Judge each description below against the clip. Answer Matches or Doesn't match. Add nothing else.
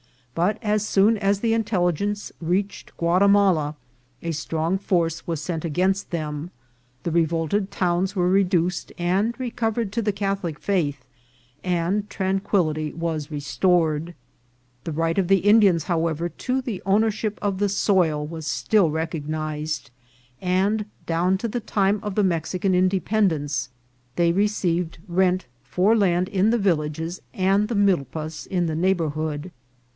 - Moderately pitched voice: Matches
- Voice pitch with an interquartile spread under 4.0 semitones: Matches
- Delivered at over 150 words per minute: Doesn't match